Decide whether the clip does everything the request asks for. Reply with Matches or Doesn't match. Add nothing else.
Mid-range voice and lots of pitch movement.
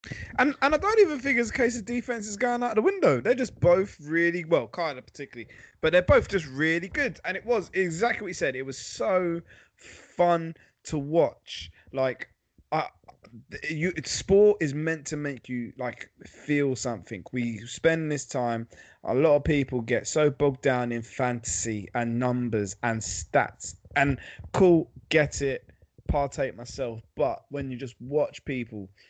Matches